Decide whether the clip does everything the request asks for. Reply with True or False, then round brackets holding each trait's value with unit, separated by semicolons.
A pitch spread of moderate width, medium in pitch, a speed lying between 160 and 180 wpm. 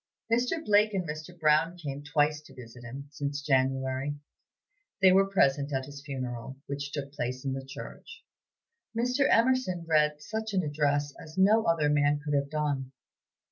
True (4.5 semitones; 150 Hz; 165 wpm)